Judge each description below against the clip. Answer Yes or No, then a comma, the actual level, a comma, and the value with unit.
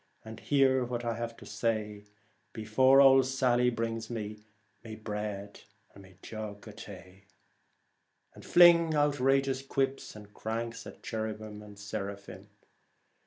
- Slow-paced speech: Yes, slow, 125 wpm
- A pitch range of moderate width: Yes, average, 3.8 semitones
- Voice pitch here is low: Yes, low, 115 Hz